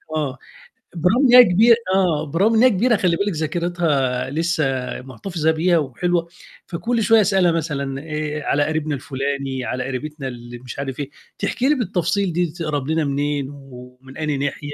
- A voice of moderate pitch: Yes, medium, 155 Hz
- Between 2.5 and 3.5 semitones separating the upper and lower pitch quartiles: No, average, 4.5 semitones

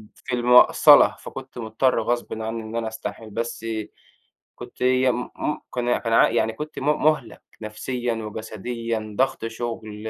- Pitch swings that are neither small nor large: No, narrow, 1.9 semitones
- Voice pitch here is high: No, low, 115 Hz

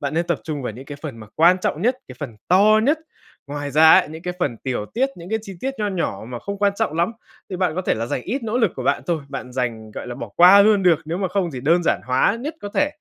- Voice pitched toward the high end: No, medium, 170 Hz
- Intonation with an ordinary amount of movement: No, wide, 6.6 semitones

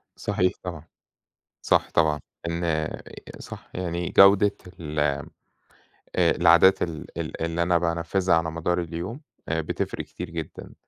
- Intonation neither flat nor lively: No, narrow, 1.6 semitones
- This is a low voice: Yes, very low, 85 Hz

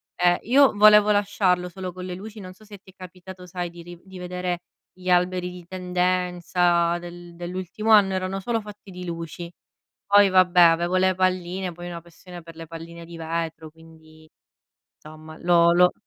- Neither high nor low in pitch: Yes, medium, 180 Hz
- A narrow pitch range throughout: Yes, narrow, 1.6 semitones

